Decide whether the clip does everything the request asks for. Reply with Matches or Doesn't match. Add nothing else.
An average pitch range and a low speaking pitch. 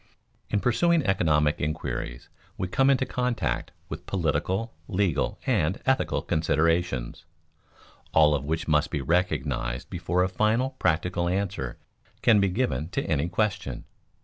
Doesn't match